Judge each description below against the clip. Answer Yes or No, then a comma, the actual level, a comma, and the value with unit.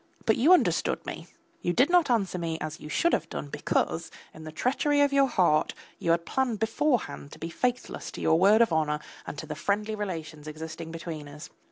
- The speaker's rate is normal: No, fast, 210 wpm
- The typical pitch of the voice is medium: Yes, medium, 175 Hz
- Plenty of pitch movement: Yes, wide, 7.8 semitones